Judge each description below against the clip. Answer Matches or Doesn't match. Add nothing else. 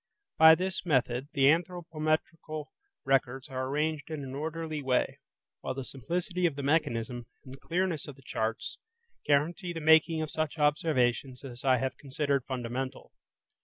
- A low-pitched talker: Doesn't match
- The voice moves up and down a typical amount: Matches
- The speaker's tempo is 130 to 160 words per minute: Matches